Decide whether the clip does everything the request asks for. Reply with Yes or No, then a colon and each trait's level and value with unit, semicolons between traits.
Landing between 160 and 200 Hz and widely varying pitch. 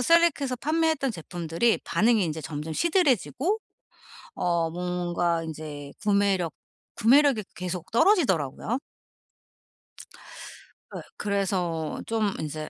Yes: high, 190 Hz; wide, 7.5 semitones